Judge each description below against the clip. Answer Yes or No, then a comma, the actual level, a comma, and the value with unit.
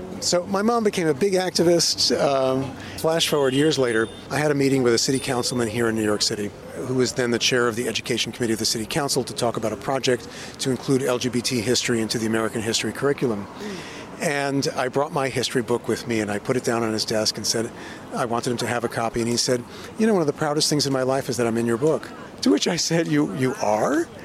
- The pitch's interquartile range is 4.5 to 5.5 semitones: No, average, 3.5 semitones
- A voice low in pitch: Yes, low, 125 Hz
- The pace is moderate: No, fast, 255 wpm